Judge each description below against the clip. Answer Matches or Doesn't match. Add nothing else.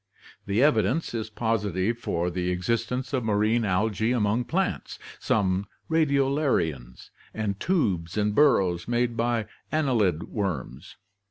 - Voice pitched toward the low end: Matches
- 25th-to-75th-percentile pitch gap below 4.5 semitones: Doesn't match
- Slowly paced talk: Matches